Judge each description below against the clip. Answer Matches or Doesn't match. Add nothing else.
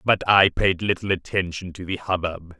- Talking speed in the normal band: Matches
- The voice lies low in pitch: Matches